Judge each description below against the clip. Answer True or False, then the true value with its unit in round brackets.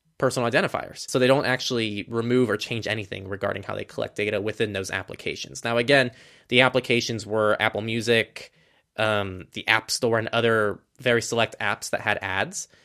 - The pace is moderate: True (175 wpm)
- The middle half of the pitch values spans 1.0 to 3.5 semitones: True (2.9 semitones)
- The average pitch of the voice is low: True (115 Hz)